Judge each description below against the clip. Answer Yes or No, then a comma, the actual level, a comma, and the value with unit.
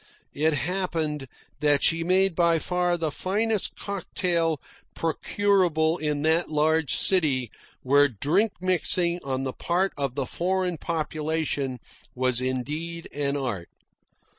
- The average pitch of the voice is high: No, medium, 160 Hz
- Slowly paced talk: Yes, slow, 120 wpm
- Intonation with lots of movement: No, average, 3.8 semitones